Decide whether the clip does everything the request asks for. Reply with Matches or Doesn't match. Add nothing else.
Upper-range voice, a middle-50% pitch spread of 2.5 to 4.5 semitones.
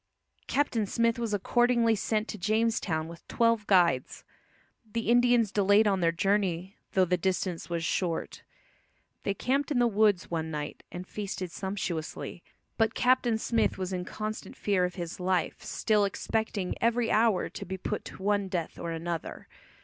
Matches